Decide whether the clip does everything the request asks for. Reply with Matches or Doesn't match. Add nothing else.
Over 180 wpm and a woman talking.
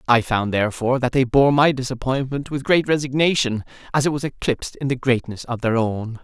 Doesn't match